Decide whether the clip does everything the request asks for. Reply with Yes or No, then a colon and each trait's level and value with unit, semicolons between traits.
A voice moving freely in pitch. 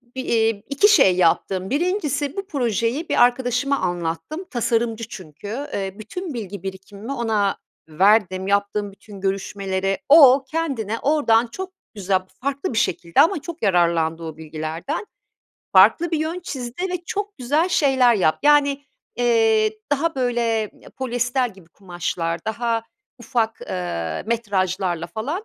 Yes: wide, 6.6 semitones